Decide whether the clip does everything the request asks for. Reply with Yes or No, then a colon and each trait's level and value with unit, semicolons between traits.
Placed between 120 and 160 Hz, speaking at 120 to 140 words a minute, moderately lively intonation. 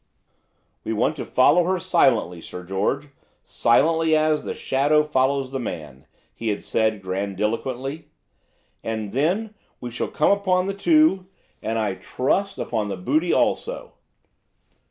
No: low, 135 Hz; slow, 135 wpm; wide, 7.3 semitones